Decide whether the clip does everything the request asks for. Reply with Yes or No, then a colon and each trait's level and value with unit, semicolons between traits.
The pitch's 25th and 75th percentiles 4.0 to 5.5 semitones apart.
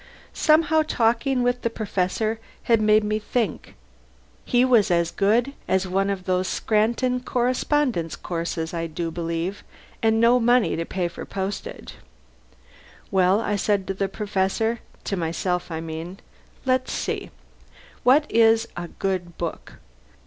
Yes: average, 4.7 semitones